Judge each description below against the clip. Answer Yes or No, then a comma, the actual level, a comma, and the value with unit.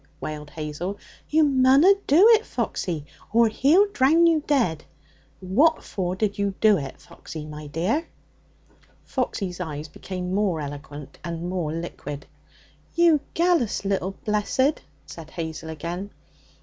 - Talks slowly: Yes, slow, 130 wpm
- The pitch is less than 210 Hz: Yes, high, 190 Hz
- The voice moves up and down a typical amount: No, wide, 9.0 semitones